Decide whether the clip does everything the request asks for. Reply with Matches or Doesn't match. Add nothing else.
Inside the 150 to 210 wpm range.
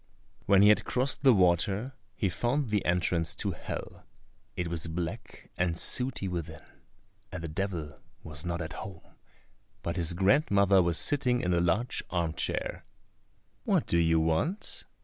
Matches